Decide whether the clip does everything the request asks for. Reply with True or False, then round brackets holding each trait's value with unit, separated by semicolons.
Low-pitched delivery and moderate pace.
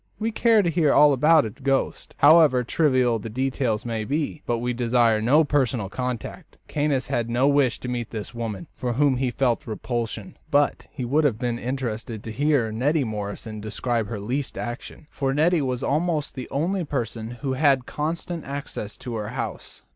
True (125 Hz; 185 wpm)